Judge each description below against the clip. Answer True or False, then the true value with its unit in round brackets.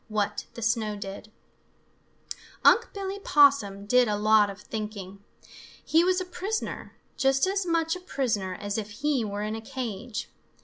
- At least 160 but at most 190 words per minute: True (165 wpm)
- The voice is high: True (225 Hz)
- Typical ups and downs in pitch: False (7.2 semitones)